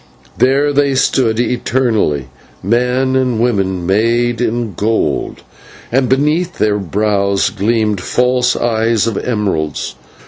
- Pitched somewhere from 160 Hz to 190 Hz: No, low, 115 Hz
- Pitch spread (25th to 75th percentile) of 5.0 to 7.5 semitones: No, average, 3.5 semitones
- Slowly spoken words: Yes, slow, 110 wpm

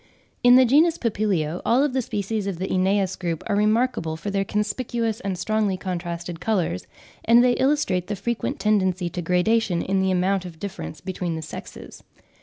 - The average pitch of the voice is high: Yes, high, 195 Hz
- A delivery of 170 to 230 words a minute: Yes, average, 175 wpm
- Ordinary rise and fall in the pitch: Yes, average, 4.0 semitones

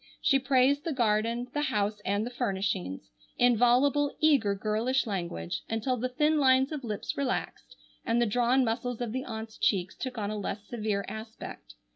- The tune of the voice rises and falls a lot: No, average, 3.7 semitones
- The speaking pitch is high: Yes, high, 235 Hz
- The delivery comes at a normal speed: Yes, average, 175 wpm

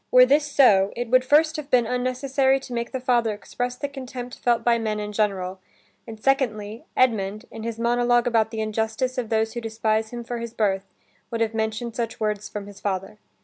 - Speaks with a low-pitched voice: No, high, 230 Hz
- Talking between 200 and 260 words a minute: Yes, fast, 205 wpm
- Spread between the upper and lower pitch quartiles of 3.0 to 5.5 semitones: No, narrow, 2.6 semitones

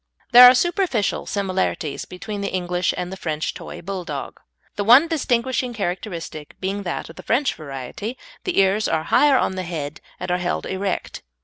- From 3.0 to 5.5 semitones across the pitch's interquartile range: Yes, average, 5.2 semitones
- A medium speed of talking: Yes, average, 175 wpm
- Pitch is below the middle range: No, high, 190 Hz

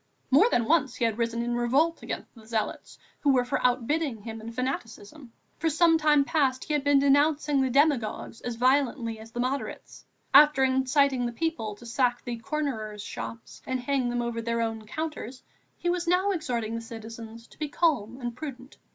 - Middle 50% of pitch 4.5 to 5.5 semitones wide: No, average, 4.0 semitones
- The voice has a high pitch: Yes, very high, 255 Hz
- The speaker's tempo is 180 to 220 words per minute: Yes, average, 190 wpm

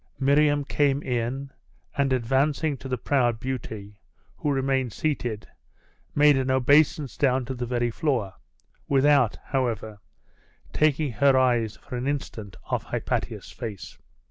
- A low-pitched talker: Yes, low, 130 Hz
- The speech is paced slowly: Yes, slow, 130 wpm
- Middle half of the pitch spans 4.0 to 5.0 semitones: No, average, 3.0 semitones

